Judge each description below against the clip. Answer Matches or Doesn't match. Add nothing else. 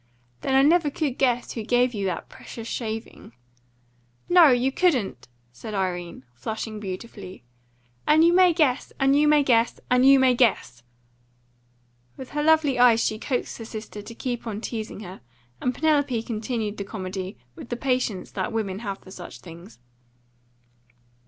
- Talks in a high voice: Matches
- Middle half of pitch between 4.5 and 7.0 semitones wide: Matches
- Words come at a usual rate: Matches